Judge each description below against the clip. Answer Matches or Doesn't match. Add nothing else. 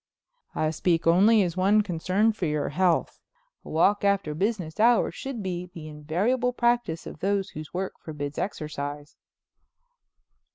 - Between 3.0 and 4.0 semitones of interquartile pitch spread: Doesn't match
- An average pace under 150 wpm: Matches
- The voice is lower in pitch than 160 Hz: Doesn't match